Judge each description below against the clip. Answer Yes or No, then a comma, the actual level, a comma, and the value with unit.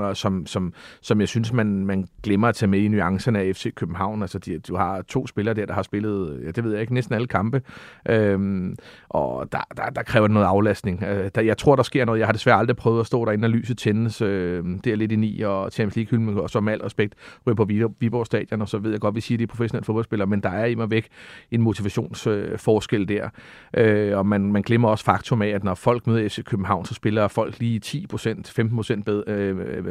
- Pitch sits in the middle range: No, low, 110 Hz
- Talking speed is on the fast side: Yes, fast, 240 wpm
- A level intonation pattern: Yes, narrow, 2.3 semitones